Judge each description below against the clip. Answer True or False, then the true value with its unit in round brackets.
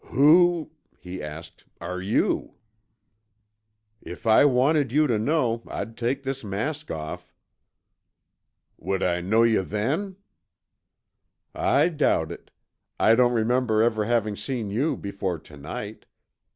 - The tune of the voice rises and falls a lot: True (6.0 semitones)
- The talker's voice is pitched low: True (115 Hz)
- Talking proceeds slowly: True (120 wpm)